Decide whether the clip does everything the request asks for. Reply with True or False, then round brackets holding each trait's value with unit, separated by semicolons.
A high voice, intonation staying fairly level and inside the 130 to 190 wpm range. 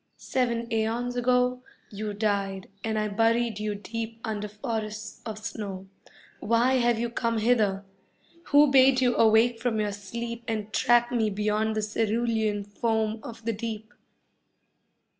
True (225 Hz; 2.0 semitones; 140 wpm)